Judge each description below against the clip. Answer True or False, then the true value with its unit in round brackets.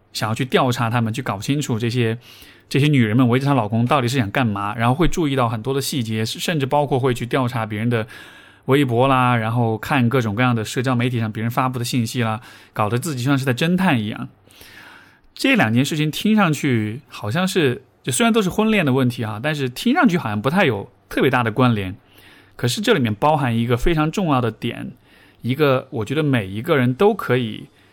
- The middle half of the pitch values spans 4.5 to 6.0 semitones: False (3.9 semitones)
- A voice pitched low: True (125 Hz)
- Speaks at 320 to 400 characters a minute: True (325 characters per minute)